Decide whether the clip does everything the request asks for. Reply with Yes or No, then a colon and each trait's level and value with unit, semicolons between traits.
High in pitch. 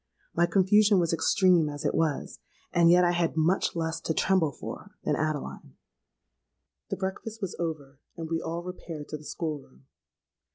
No: medium, 165 Hz